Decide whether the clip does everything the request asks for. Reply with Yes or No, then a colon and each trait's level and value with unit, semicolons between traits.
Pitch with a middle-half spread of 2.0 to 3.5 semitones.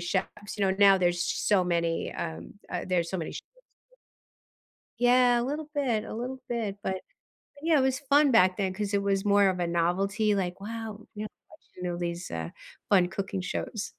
No: average, 4.3 semitones